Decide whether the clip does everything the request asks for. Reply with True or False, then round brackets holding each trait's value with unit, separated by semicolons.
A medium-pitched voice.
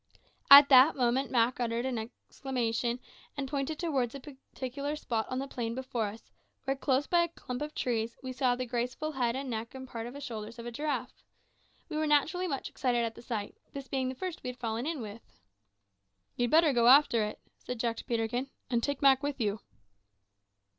False (255 Hz)